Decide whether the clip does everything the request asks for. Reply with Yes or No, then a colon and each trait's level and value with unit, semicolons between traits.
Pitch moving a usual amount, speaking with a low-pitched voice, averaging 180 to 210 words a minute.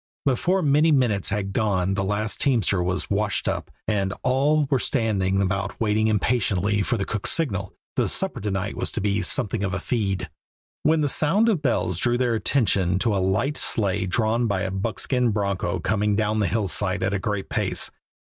Yes: average, 3.8 semitones; low, 105 Hz; average, 190 wpm